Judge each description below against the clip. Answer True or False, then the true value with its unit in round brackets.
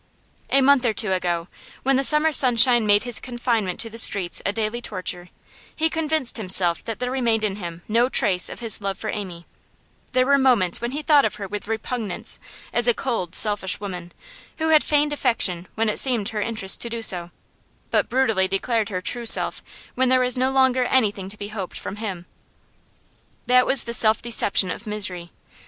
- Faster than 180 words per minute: True (195 wpm)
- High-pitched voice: True (225 Hz)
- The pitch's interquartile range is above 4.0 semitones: True (4.6 semitones)